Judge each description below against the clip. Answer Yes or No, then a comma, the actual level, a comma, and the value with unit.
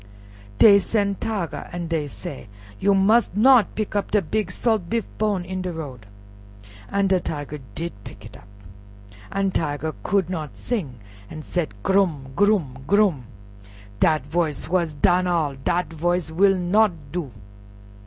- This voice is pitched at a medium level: Yes, medium, 175 Hz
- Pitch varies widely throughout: No, average, 4.6 semitones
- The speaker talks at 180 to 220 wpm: No, average, 155 wpm